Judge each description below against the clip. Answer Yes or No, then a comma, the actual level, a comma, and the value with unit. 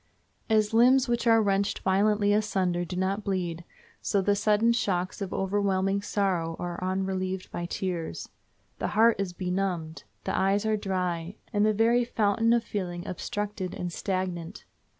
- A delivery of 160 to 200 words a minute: No, average, 150 wpm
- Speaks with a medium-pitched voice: No, high, 195 Hz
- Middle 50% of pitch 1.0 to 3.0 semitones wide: Yes, narrow, 2.6 semitones